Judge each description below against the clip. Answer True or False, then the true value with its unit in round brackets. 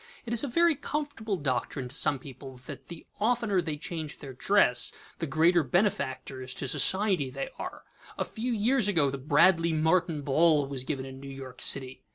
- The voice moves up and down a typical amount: False (6.9 semitones)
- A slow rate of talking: False (185 wpm)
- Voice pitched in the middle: True (155 Hz)